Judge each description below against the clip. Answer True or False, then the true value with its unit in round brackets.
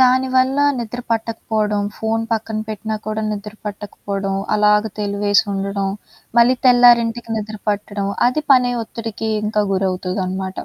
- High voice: True (215 Hz)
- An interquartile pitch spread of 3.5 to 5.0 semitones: False (2.4 semitones)